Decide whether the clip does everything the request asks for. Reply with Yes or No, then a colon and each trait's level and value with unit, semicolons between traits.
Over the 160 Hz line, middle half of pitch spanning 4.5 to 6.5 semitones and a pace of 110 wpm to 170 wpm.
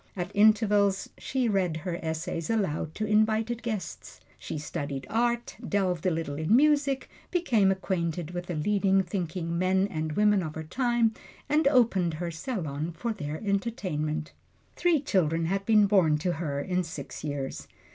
Yes: medium, 185 Hz; average, 5.2 semitones; average, 155 wpm